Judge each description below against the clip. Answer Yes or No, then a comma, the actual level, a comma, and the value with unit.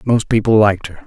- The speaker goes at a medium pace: No, fast, 225 wpm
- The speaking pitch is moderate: No, low, 105 Hz